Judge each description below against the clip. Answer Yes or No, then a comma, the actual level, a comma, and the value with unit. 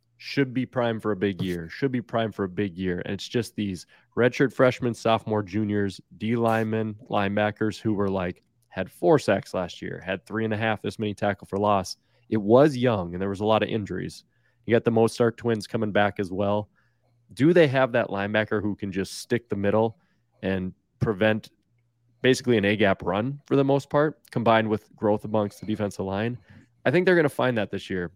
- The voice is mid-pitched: No, low, 110 Hz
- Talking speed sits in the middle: No, fast, 210 wpm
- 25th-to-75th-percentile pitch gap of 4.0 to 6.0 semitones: No, average, 2.8 semitones